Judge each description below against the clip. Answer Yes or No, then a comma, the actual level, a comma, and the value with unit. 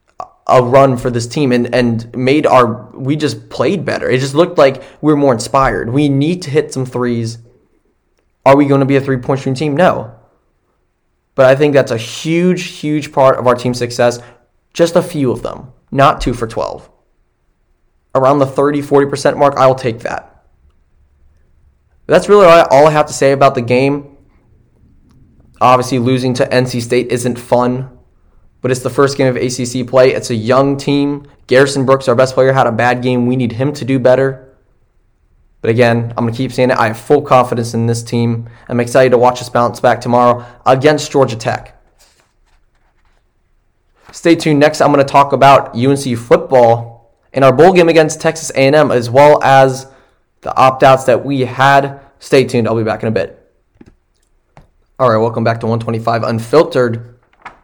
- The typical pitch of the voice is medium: No, low, 130 Hz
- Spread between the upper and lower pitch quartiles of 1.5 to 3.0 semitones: Yes, average, 2.7 semitones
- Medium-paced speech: Yes, average, 185 wpm